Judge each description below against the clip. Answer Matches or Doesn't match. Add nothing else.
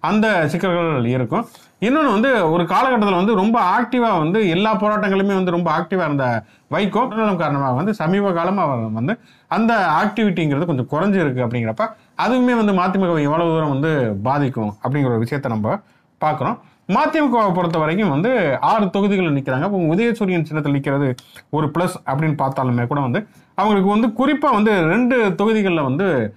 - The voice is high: Doesn't match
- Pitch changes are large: Matches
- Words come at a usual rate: Doesn't match